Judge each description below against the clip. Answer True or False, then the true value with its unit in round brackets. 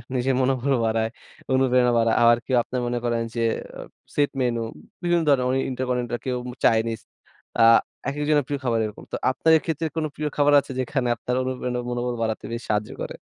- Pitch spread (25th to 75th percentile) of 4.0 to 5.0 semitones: False (2.5 semitones)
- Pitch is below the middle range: True (125 Hz)